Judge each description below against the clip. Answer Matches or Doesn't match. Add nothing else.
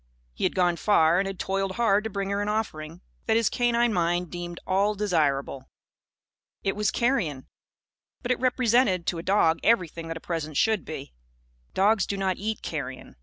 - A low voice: Doesn't match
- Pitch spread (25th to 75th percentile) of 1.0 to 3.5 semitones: Doesn't match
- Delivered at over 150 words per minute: Matches